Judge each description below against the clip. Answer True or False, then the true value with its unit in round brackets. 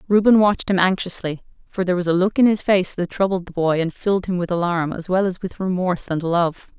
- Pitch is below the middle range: False (180 Hz)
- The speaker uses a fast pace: True (245 wpm)